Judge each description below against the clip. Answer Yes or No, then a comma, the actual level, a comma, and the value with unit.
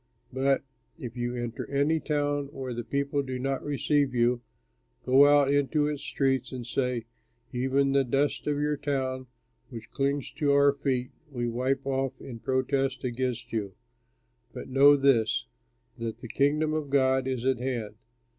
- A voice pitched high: No, low, 135 Hz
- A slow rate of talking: No, average, 160 wpm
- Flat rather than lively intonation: Yes, narrow, 2.1 semitones